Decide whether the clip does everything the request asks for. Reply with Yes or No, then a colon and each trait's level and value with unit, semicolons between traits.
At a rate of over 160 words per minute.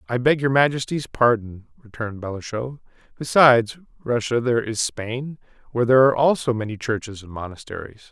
No: average, 150 wpm